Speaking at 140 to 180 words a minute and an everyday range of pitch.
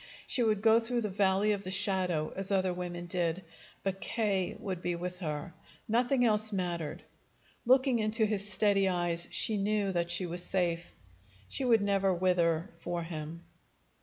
Yes: average, 165 wpm; average, 3.4 semitones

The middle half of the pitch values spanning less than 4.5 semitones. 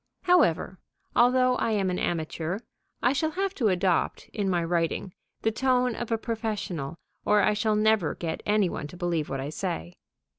No: wide, 5.4 semitones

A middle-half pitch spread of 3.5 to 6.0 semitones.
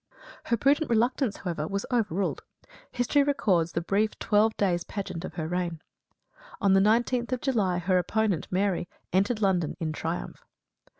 Yes: average, 4.6 semitones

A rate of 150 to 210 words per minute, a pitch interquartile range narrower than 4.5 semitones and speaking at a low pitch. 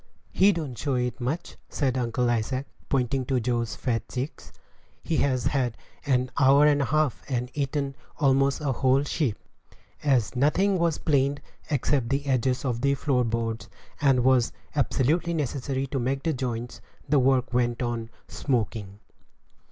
Yes: average, 160 wpm; narrow, 2.6 semitones; low, 130 Hz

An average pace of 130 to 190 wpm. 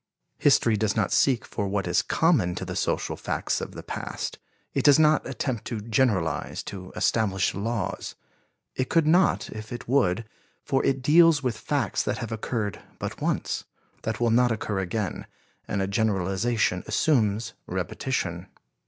Yes: average, 160 wpm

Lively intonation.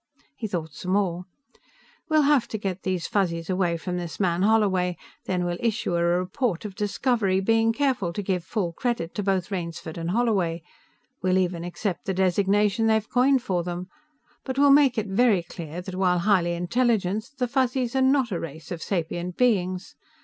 No: average, 4.3 semitones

